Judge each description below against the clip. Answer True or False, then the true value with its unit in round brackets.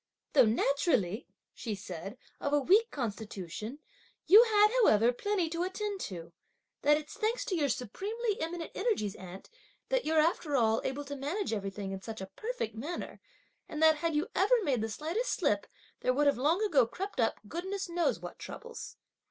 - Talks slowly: False (175 wpm)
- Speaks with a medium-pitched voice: False (295 Hz)